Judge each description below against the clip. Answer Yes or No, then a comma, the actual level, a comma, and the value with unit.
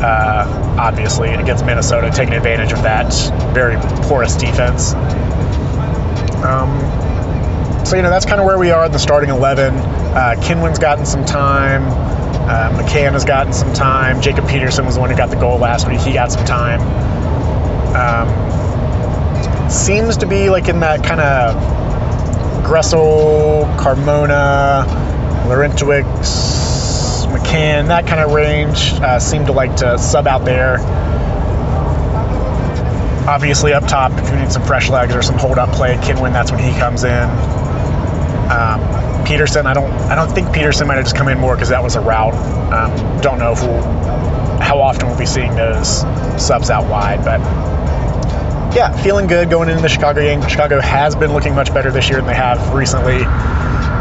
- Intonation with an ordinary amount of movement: Yes, average, 4.5 semitones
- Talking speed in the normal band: Yes, average, 165 wpm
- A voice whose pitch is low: Yes, low, 125 Hz